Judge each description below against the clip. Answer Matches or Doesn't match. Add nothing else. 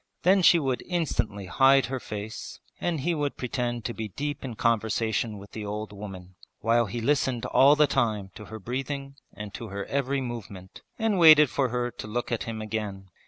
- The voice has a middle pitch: Doesn't match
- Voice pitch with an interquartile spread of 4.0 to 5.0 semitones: Matches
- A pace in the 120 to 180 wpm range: Doesn't match